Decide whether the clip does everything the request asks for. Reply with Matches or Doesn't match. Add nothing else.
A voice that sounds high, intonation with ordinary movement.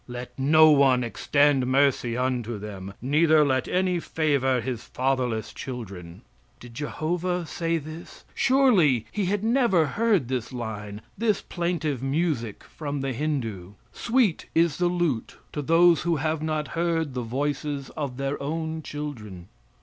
Doesn't match